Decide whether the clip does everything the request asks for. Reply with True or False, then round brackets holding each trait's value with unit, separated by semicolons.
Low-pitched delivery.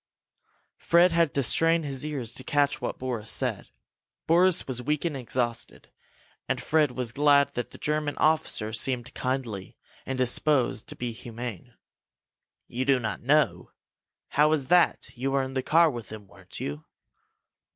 True (130 Hz)